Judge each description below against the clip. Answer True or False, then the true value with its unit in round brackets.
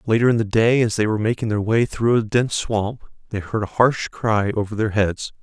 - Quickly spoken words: True (245 wpm)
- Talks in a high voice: False (110 Hz)